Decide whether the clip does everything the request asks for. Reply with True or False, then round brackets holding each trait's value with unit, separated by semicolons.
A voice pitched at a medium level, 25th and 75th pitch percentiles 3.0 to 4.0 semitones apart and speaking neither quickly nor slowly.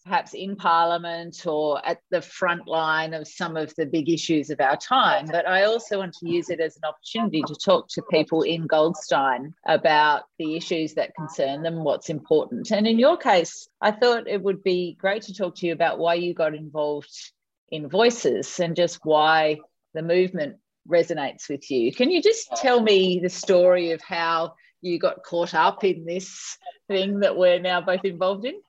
True (175 Hz; 3.6 semitones; 190 wpm)